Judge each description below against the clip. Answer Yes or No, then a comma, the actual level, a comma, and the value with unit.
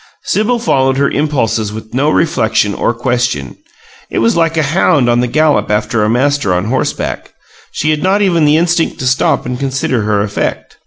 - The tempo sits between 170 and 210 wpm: Yes, average, 190 wpm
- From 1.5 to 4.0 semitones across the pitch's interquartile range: No, wide, 5.4 semitones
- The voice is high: No, low, 130 Hz